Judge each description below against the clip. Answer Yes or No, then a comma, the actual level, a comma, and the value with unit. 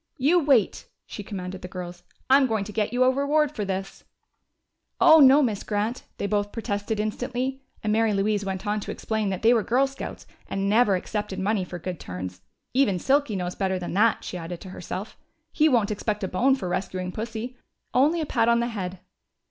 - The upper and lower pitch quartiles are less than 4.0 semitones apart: No, average, 4.6 semitones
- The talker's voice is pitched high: Yes, high, 210 Hz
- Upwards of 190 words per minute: Yes, fast, 205 wpm